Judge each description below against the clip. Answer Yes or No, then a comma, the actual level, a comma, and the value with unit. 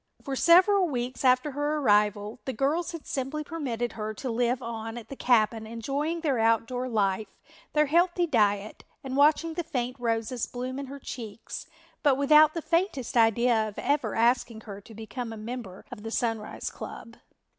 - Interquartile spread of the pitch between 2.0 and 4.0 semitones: No, average, 4.4 semitones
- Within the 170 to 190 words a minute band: Yes, average, 175 wpm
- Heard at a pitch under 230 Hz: No, high, 245 Hz